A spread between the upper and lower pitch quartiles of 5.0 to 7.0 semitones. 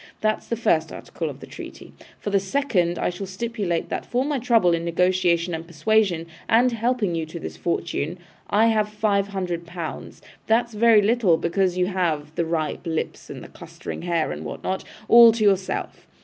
No: average, 4.4 semitones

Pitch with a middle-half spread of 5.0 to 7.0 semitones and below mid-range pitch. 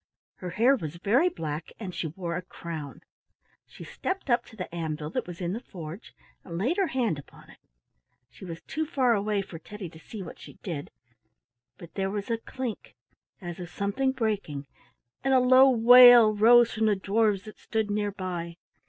No: wide, 5.6 semitones; high, 205 Hz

